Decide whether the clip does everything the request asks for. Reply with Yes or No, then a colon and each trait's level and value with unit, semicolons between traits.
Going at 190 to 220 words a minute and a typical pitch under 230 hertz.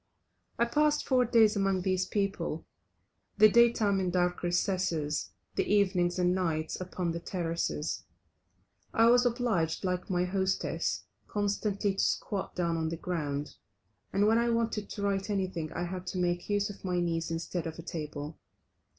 No: average, 165 wpm; medium, 185 Hz